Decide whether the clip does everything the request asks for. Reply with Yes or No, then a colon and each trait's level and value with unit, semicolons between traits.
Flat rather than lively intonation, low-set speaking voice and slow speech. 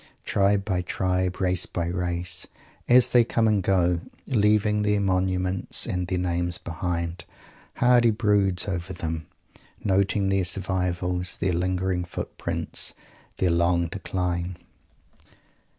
Yes: narrow, 2.0 semitones; very low, 95 Hz; slow, 120 wpm